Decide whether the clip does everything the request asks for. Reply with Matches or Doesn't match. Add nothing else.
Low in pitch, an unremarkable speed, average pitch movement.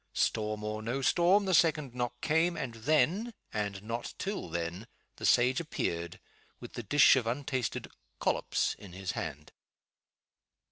Doesn't match